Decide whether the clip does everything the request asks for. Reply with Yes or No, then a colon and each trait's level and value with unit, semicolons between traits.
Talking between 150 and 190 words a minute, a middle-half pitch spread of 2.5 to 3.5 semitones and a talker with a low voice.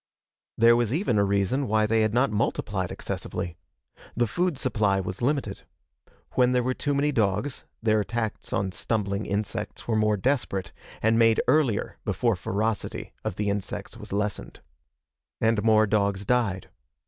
Yes: average, 155 wpm; average, 3.2 semitones; low, 110 Hz